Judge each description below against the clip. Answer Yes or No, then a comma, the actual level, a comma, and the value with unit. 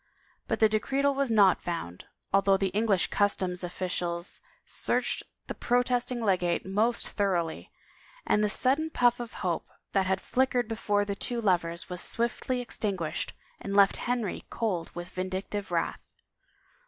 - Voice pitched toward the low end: No, high, 200 Hz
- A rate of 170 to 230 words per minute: No, average, 145 wpm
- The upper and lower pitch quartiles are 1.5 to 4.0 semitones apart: No, average, 4.4 semitones